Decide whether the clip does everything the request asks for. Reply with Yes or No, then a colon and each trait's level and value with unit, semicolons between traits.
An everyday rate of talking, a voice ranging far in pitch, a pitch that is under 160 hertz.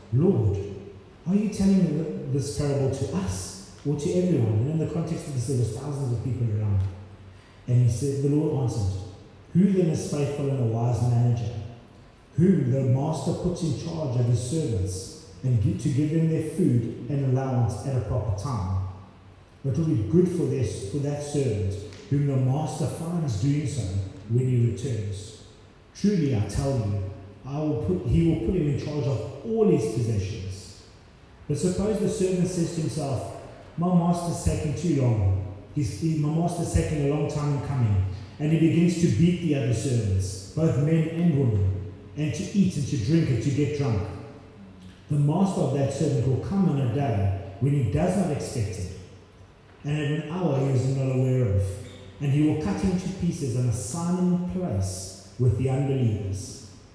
Yes: average, 190 wpm; wide, 6.5 semitones; low, 135 Hz